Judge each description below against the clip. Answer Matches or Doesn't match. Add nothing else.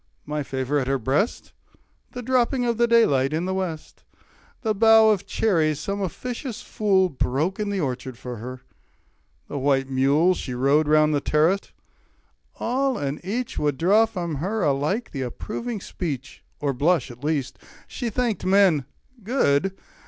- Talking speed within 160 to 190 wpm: Matches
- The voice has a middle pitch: Matches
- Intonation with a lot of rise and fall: Matches